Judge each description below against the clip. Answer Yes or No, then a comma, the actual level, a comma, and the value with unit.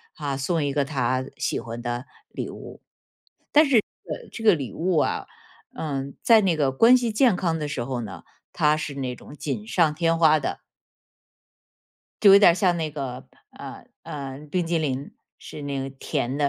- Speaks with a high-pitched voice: No, medium, 150 Hz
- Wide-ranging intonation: No, average, 4.4 semitones